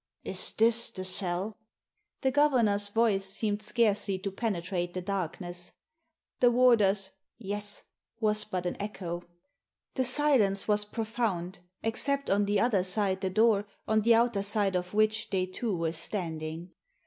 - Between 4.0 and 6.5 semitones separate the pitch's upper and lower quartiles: No, average, 3.1 semitones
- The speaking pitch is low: No, high, 205 Hz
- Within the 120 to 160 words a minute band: Yes, average, 150 wpm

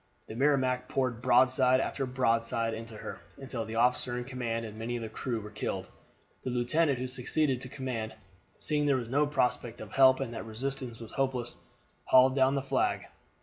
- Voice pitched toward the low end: Yes, low, 125 Hz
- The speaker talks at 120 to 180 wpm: No, average, 190 wpm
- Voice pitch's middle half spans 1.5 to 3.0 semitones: Yes, narrow, 2.5 semitones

